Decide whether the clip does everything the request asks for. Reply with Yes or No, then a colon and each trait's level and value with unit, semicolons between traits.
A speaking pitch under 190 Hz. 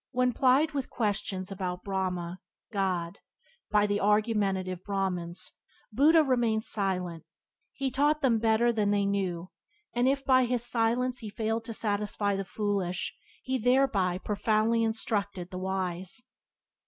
No: high, 210 Hz